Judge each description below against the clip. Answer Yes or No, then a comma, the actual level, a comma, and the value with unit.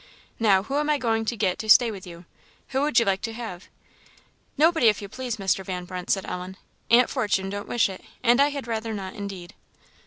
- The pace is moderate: No, fast, 220 wpm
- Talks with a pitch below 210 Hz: No, high, 215 Hz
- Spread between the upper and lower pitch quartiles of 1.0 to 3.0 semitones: No, average, 4.1 semitones